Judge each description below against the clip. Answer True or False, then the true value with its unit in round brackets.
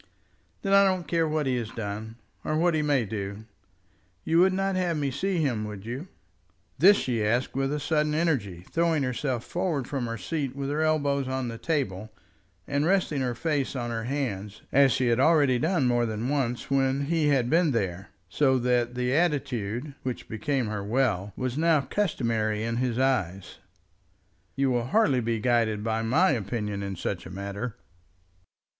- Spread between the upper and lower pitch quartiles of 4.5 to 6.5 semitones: True (5.0 semitones)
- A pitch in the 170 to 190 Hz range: False (130 Hz)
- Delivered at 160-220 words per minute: True (180 wpm)